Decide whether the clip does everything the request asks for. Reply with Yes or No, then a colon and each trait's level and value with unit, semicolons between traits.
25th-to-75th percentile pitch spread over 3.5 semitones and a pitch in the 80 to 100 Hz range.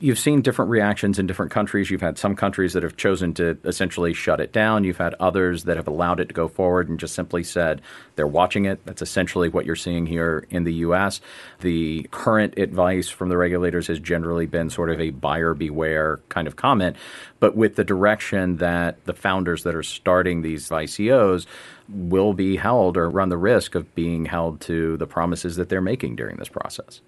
No: narrow, 2.4 semitones; very low, 90 Hz